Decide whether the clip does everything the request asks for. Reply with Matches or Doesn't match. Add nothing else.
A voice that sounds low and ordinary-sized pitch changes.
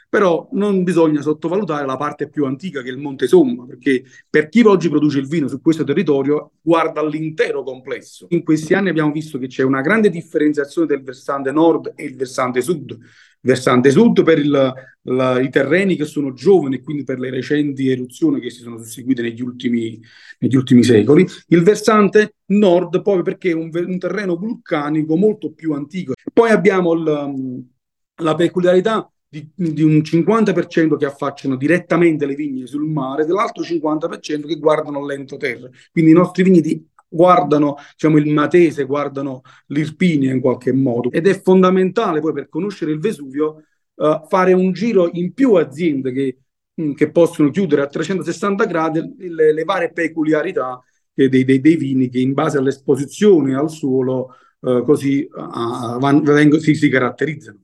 Doesn't match